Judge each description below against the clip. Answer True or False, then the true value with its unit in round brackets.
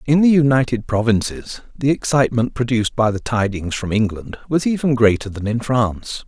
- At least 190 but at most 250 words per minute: False (170 wpm)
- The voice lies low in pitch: True (120 Hz)